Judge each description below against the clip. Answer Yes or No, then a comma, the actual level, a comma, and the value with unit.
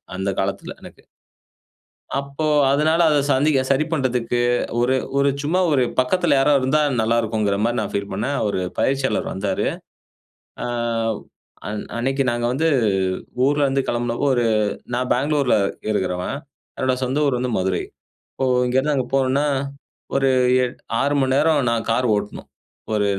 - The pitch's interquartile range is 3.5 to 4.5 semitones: No, average, 3.1 semitones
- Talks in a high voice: No, low, 130 Hz